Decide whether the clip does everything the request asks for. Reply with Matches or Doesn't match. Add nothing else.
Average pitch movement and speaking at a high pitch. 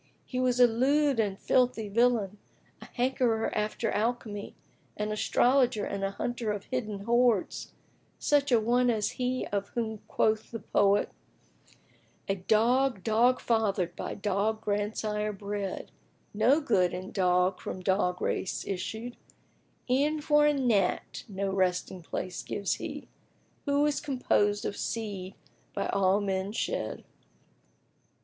Matches